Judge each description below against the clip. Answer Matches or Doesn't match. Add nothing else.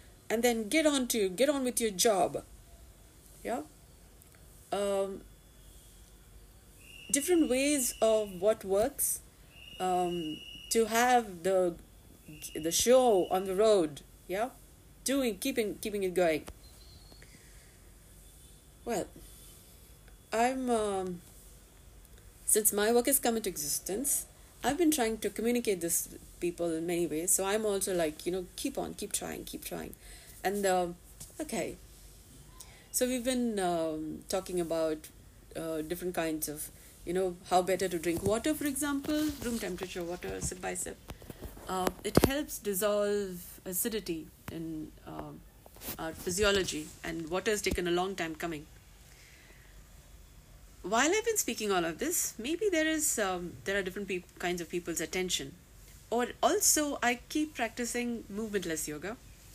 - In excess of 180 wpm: Doesn't match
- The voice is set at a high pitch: Matches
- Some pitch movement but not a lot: Doesn't match